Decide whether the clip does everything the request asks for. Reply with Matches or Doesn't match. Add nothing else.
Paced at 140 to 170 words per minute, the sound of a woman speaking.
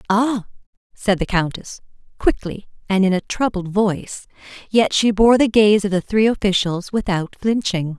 Matches